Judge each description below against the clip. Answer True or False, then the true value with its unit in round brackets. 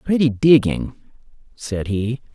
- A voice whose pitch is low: True (125 Hz)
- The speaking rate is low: True (100 wpm)